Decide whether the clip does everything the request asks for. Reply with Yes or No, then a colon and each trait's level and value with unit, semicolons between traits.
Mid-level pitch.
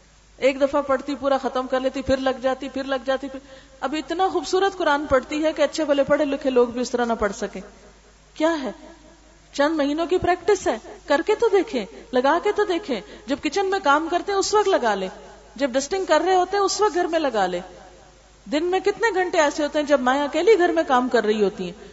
No: very high, 285 Hz